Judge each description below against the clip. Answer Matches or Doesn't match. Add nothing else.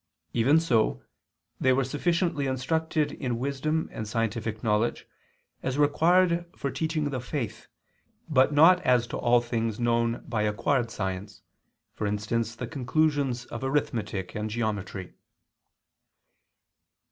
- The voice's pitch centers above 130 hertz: Doesn't match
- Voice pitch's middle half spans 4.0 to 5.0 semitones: Matches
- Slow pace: Matches